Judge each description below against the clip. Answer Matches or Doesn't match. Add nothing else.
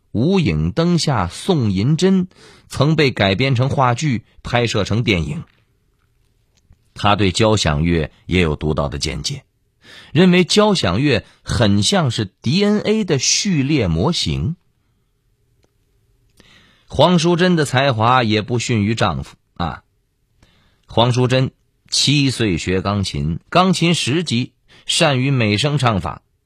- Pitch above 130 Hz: Doesn't match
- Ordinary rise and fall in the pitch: Doesn't match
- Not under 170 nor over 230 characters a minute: Matches